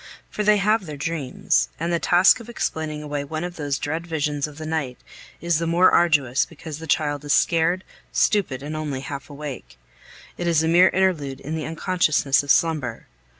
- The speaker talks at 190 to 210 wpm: Yes, average, 195 wpm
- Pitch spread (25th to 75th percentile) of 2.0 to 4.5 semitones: Yes, average, 3.0 semitones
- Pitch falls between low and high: Yes, medium, 155 Hz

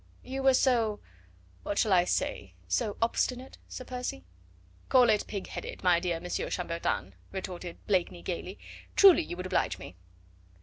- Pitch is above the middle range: Yes, high, 195 Hz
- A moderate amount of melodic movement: No, wide, 6.0 semitones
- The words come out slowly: No, average, 150 wpm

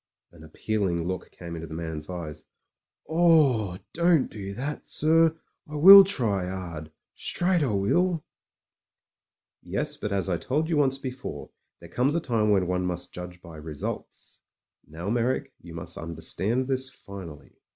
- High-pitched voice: No, low, 105 Hz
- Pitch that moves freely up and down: Yes, wide, 8.6 semitones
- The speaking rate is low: No, average, 155 wpm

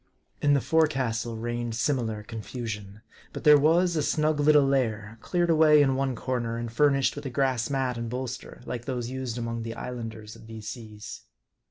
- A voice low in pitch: Yes, low, 125 Hz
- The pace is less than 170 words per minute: No, average, 185 wpm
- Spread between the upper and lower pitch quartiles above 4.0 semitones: No, average, 3.7 semitones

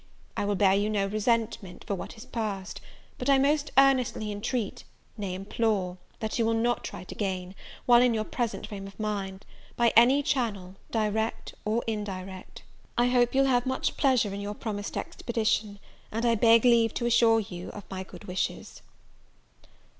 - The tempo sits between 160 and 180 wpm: Yes, average, 175 wpm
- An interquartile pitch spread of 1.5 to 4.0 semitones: Yes, average, 3.2 semitones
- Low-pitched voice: No, high, 220 Hz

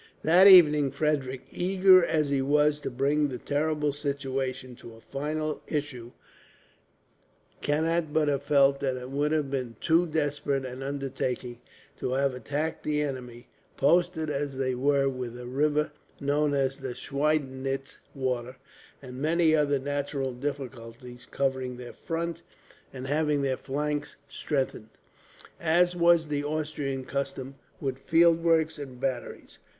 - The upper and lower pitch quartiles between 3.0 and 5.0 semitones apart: No, narrow, 2.5 semitones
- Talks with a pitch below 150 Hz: Yes, medium, 140 Hz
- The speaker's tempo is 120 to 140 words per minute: Yes, slow, 135 wpm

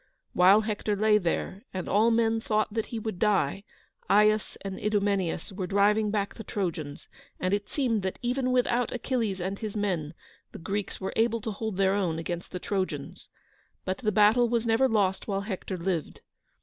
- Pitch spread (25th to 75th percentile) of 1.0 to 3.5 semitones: Yes, average, 2.7 semitones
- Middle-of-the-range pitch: No, high, 205 Hz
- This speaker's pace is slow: No, average, 180 wpm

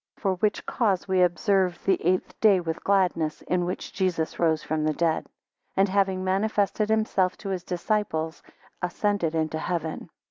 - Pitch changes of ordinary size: Yes, average, 3.1 semitones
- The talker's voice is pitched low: No, medium, 185 Hz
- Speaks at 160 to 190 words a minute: Yes, average, 165 wpm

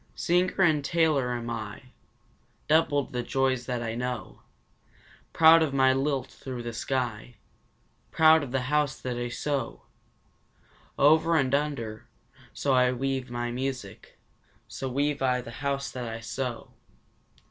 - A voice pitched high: No, low, 130 Hz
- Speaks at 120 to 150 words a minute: Yes, average, 140 wpm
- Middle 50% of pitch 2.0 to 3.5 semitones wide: Yes, average, 2.9 semitones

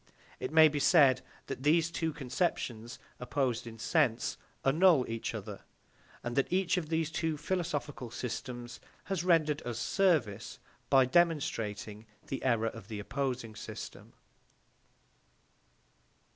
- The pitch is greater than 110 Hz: Yes, low, 135 Hz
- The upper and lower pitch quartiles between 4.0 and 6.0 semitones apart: Yes, average, 5.3 semitones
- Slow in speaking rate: Yes, slow, 125 wpm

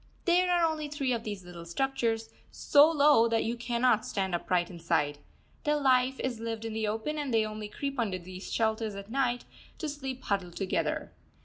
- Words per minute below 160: No, average, 190 wpm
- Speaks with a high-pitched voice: Yes, high, 230 Hz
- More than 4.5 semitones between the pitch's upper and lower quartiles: Yes, average, 5.2 semitones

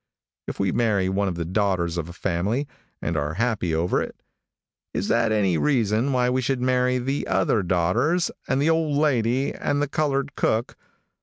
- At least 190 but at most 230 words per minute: No, average, 180 wpm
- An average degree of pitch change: No, wide, 6.5 semitones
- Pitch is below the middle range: Yes, low, 115 Hz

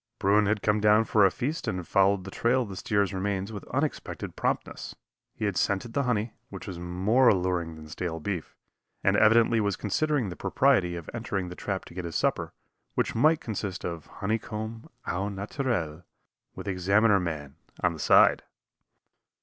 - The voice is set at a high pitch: No, low, 100 Hz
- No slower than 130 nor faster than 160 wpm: No, average, 180 wpm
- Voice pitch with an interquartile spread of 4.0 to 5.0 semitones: No, average, 3.6 semitones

